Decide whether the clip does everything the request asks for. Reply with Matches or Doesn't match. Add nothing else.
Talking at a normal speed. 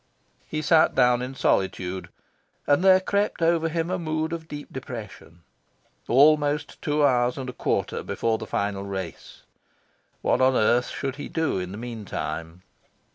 Matches